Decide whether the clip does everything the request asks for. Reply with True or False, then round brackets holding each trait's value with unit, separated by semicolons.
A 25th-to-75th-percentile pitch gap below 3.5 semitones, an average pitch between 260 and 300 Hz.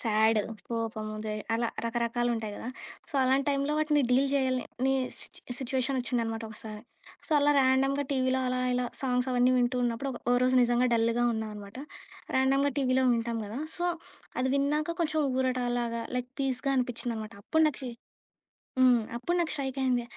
False (2.6 semitones; 250 Hz)